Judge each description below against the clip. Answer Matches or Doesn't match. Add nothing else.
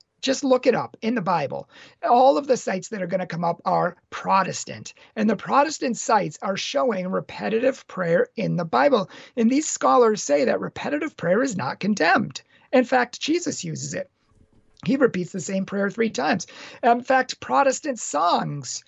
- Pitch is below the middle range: Doesn't match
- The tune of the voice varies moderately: Doesn't match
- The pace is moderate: Matches